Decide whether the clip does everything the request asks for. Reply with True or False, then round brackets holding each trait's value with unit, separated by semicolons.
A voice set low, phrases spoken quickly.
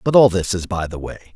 True (100 Hz; 310 wpm)